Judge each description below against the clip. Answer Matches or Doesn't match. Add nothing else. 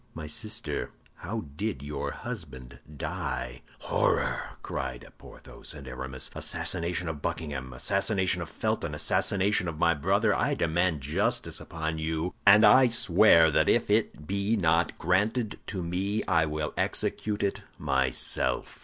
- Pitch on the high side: Doesn't match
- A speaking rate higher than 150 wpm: Doesn't match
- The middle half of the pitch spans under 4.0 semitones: Doesn't match